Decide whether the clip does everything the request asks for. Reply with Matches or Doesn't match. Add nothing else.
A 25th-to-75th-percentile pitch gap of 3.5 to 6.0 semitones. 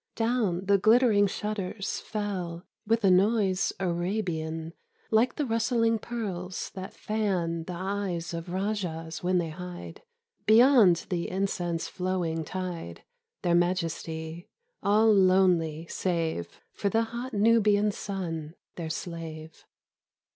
Matches